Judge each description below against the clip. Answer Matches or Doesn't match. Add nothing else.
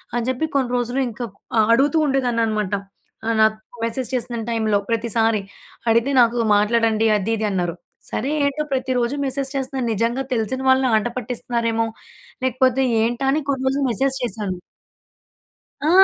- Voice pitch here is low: Doesn't match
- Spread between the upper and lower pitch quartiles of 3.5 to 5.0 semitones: Doesn't match